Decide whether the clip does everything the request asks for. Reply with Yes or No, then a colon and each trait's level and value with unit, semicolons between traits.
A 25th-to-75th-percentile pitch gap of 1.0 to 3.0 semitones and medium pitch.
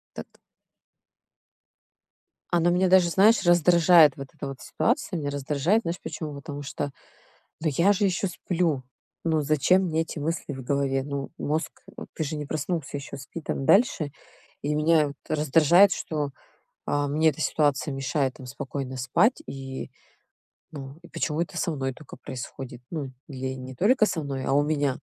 No: average, 3.6 semitones; medium, 150 Hz